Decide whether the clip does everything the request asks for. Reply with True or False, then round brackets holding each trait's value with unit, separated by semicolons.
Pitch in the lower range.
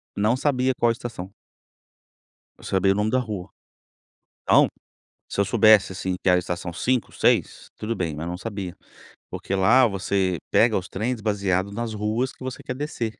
True (105 Hz)